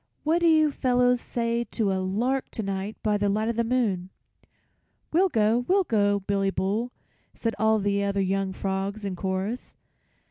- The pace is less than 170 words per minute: No, average, 175 wpm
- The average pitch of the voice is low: No, high, 215 Hz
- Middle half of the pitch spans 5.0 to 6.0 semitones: No, average, 3.7 semitones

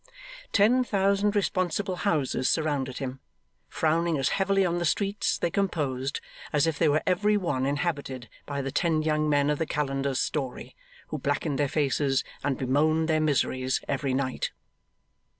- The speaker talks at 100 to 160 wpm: Yes, average, 155 wpm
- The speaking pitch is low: No, medium, 150 Hz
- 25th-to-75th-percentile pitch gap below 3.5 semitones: No, average, 4.2 semitones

